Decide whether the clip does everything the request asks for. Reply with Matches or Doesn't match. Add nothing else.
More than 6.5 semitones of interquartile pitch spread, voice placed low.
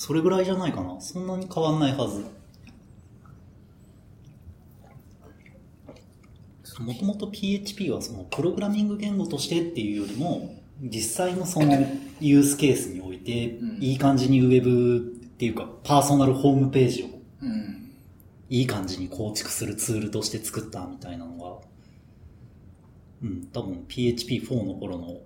Doesn't match